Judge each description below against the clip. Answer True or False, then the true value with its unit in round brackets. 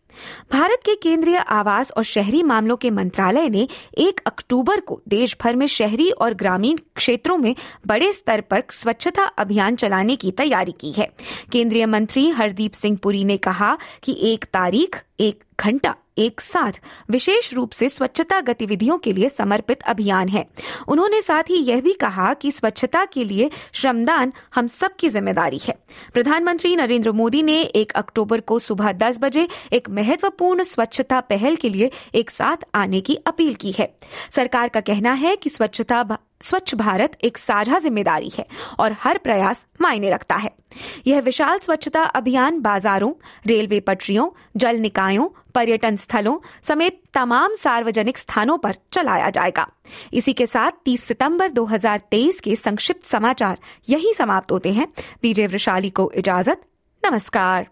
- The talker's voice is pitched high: True (240 Hz)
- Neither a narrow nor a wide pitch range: False (6.2 semitones)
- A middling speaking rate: True (155 wpm)